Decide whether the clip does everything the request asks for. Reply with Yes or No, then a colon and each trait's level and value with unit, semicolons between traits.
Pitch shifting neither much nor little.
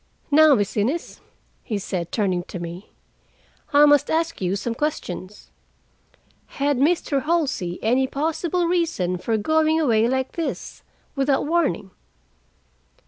No: wide, 7.4 semitones